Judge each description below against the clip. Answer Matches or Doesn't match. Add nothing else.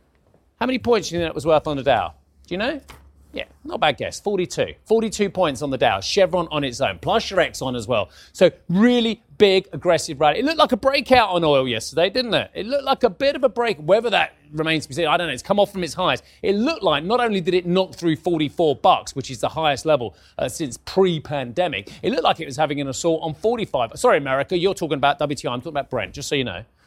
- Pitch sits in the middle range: Matches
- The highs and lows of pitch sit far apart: Matches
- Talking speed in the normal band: Doesn't match